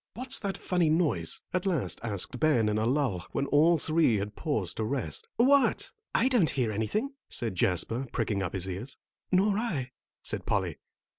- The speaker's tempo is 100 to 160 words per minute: No, average, 175 wpm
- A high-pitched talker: No, low, 135 Hz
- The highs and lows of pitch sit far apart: Yes, wide, 9.0 semitones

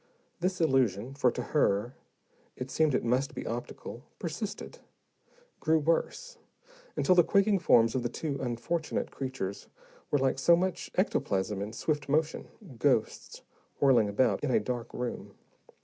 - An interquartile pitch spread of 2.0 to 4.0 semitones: No, average, 5.3 semitones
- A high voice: No, low, 135 Hz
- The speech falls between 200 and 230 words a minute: No, average, 145 wpm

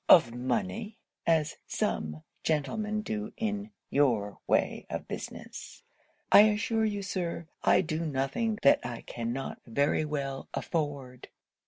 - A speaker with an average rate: No, slow, 125 wpm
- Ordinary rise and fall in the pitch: No, wide, 8.4 semitones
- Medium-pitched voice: Yes, medium, 150 Hz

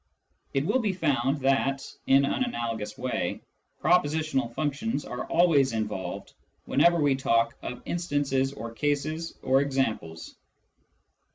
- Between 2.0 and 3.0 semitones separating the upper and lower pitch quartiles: No, average, 4.1 semitones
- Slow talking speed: Yes, slow, 120 wpm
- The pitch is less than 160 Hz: Yes, low, 135 Hz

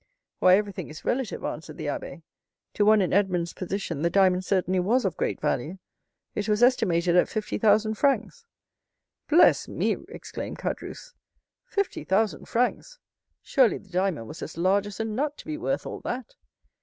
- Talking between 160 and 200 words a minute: Yes, average, 170 wpm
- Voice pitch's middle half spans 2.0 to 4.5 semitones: No, average, 4.9 semitones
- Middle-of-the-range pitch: No, high, 205 Hz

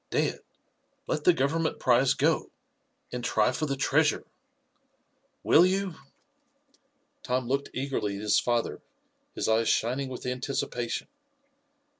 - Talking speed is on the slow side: Yes, slow, 120 wpm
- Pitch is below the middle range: Yes, low, 130 Hz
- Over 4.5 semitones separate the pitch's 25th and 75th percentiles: No, average, 2.8 semitones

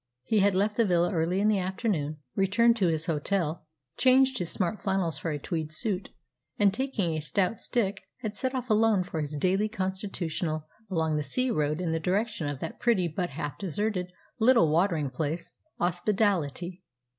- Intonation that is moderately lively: Yes, average, 4.6 semitones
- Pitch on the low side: No, medium, 185 Hz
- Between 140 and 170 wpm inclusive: No, average, 180 wpm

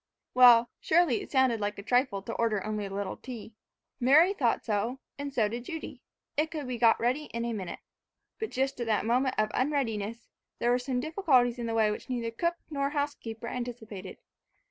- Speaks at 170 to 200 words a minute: Yes, average, 195 wpm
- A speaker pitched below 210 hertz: No, high, 240 Hz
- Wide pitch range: No, average, 3.4 semitones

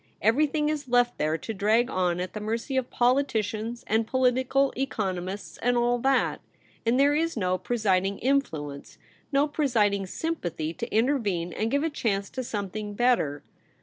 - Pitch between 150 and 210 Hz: No, high, 230 Hz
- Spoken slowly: No, average, 160 wpm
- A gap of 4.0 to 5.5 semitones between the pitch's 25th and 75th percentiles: Yes, average, 4.9 semitones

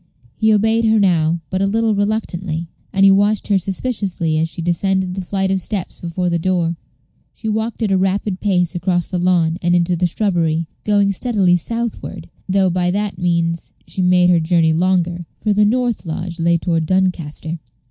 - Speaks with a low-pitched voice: No, medium, 185 Hz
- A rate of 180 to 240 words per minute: Yes, average, 185 wpm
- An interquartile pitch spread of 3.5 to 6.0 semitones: No, average, 2.9 semitones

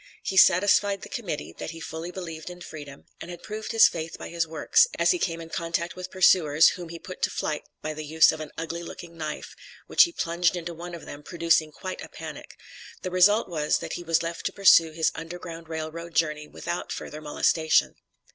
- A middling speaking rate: No, fast, 215 wpm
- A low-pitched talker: No, medium, 165 Hz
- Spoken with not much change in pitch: Yes, narrow, 2.0 semitones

